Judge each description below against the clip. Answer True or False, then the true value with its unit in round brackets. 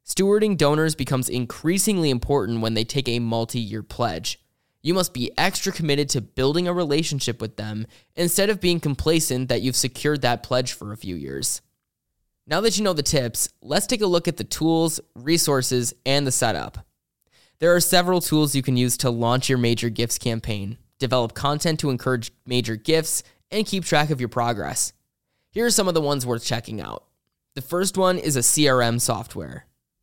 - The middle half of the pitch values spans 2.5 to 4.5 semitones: False (5.5 semitones)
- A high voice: False (130 Hz)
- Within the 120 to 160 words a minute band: False (190 wpm)